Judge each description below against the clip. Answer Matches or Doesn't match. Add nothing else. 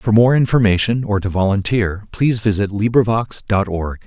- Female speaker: Doesn't match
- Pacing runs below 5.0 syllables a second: Doesn't match